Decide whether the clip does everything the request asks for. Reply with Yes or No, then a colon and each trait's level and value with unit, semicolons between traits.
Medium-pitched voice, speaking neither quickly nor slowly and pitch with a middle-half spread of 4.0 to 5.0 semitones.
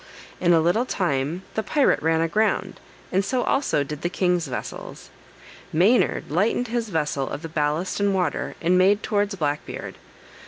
Yes: medium, 180 Hz; average, 165 wpm; average, 4.5 semitones